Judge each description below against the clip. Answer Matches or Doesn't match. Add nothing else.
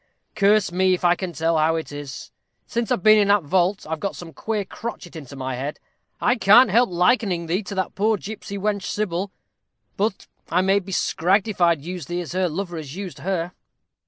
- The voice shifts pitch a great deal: Doesn't match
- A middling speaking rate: Doesn't match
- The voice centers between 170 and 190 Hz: Matches